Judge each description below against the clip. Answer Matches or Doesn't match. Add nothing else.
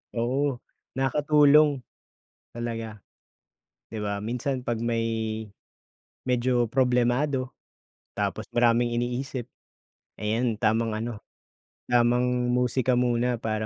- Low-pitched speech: Matches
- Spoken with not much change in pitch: Matches